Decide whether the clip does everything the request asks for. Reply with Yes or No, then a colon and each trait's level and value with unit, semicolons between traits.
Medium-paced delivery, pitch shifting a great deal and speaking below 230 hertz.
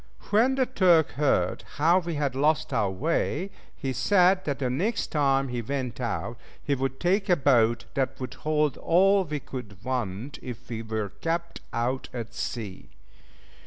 Yes: average, 165 wpm; wide, 5.7 semitones; medium, 140 Hz